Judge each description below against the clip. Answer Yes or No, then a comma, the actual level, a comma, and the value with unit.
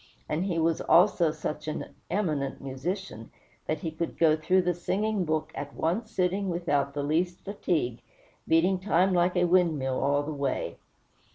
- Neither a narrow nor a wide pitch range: Yes, average, 3.4 semitones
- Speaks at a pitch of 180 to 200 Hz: No, medium, 165 Hz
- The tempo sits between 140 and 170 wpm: Yes, average, 165 wpm